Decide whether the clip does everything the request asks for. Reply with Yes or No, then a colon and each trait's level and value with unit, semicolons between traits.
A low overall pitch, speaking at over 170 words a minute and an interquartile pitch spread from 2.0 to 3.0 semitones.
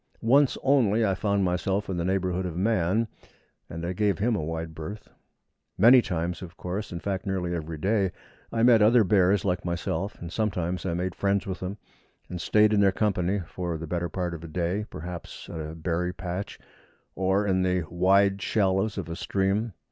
Yes: very low, 95 Hz; average, 195 wpm; average, 2.7 semitones